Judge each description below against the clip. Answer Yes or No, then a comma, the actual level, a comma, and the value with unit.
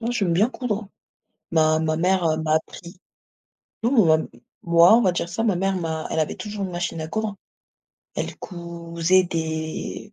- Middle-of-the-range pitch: Yes, medium, 175 Hz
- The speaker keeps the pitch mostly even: No, average, 3.6 semitones